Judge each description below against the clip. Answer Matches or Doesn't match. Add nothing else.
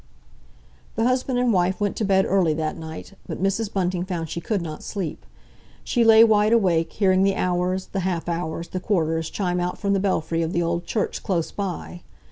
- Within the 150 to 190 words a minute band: Doesn't match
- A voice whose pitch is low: Doesn't match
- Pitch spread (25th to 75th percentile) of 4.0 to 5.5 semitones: Doesn't match